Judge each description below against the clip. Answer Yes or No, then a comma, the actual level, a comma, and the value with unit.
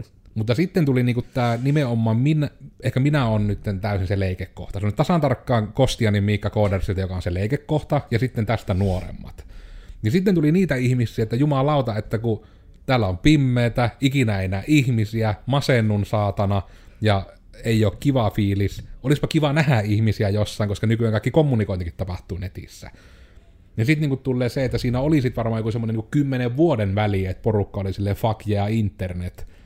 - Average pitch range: Yes, average, 4.4 semitones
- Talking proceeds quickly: Yes, fast, 170 wpm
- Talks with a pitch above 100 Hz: Yes, low, 110 Hz